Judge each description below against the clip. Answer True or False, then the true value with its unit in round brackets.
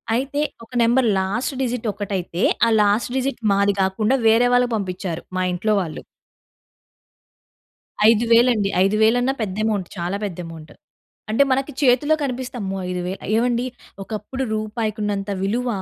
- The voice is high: True (215 Hz)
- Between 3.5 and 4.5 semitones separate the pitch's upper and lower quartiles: True (4.1 semitones)